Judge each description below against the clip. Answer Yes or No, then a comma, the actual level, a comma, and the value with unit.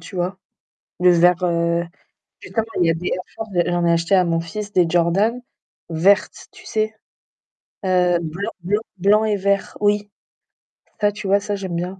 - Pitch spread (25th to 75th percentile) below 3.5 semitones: Yes, average, 3.1 semitones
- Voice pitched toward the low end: No, medium, 185 Hz